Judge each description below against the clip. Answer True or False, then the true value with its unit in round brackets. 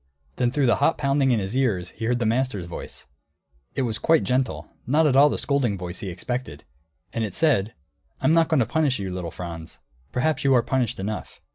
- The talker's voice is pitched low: True (125 Hz)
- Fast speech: True (215 wpm)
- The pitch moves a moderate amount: False (5.9 semitones)